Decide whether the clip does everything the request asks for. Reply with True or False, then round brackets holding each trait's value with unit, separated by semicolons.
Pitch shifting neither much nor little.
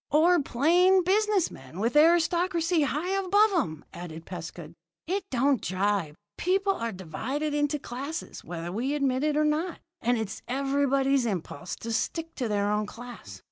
False (8.2 semitones)